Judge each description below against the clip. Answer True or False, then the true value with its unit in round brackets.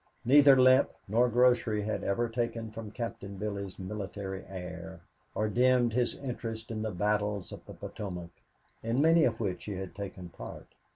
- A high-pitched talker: False (110 Hz)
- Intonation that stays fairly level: False (3.4 semitones)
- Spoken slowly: False (165 wpm)